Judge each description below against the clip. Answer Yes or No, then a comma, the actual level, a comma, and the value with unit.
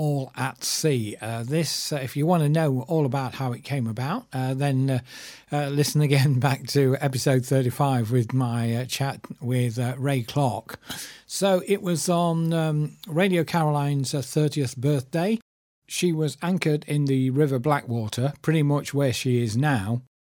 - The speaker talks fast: No, average, 170 wpm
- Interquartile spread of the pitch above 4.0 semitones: No, average, 3.0 semitones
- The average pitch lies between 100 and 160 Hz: Yes, medium, 140 Hz